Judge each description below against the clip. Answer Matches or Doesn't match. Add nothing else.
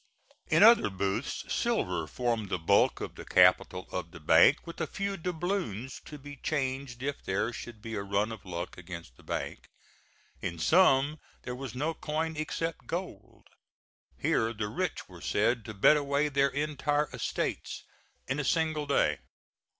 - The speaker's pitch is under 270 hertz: Matches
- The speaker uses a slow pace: Doesn't match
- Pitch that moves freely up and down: Matches